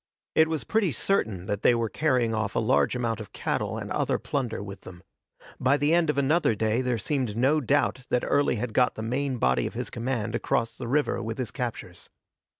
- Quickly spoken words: Yes, fast, 215 wpm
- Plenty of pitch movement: No, average, 4.3 semitones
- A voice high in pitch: No, low, 125 Hz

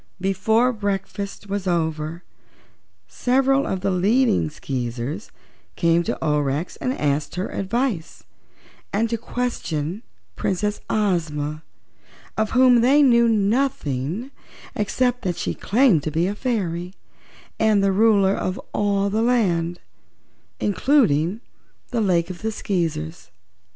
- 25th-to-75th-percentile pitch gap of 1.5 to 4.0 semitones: No, wide, 5.4 semitones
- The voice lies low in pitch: No, high, 195 Hz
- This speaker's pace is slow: Yes, slow, 120 wpm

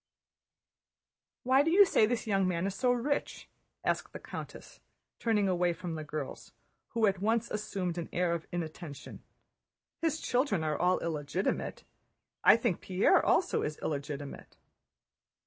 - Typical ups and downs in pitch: No, wide, 5.7 semitones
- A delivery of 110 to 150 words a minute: Yes, average, 145 wpm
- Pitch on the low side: No, medium, 185 Hz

